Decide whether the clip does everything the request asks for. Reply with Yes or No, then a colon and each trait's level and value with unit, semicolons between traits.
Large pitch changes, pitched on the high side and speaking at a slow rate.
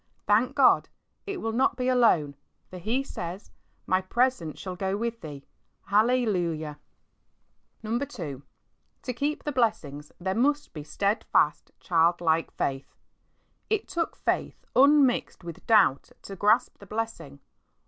Yes: wide, 6.8 semitones; high, 205 Hz; slow, 130 wpm